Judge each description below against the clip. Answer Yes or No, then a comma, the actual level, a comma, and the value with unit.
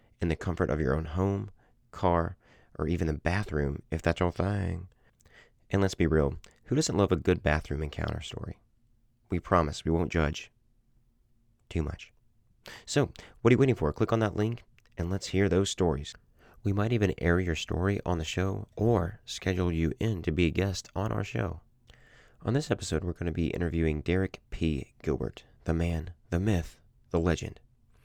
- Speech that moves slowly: No, average, 185 wpm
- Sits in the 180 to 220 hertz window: No, very low, 95 Hz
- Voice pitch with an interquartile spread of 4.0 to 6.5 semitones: Yes, average, 4.7 semitones